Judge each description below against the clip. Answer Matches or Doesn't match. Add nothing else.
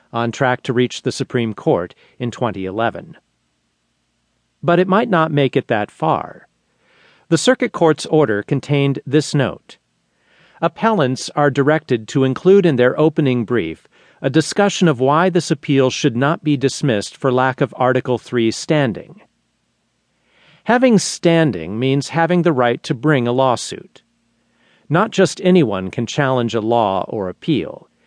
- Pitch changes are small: Doesn't match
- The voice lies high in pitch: Doesn't match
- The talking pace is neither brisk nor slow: Matches